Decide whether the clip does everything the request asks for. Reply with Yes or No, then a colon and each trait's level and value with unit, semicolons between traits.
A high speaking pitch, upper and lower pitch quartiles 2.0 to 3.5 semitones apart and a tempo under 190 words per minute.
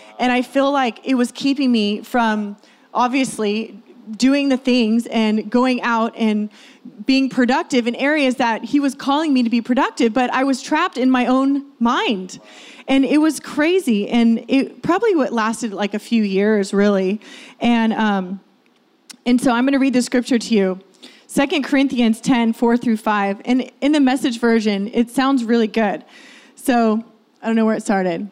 Yes: high, 245 Hz; average, 3.2 semitones; average, 180 wpm